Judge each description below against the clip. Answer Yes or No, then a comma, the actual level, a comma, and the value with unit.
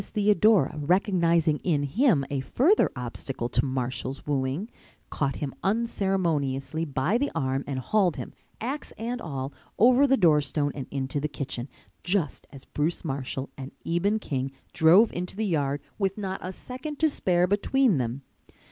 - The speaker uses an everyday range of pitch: No, wide, 6.9 semitones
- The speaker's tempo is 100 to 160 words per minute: Yes, average, 155 wpm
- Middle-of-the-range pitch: Yes, medium, 160 Hz